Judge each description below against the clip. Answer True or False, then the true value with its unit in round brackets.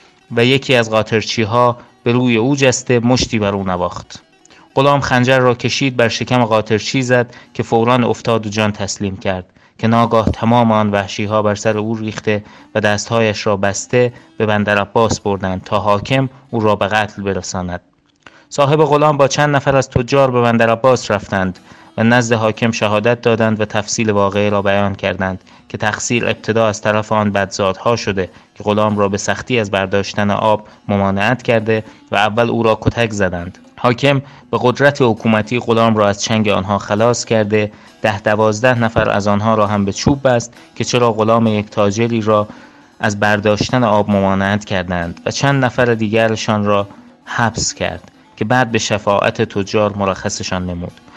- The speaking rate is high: True (170 wpm)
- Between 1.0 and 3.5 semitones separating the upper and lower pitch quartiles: True (2.8 semitones)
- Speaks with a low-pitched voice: True (110 Hz)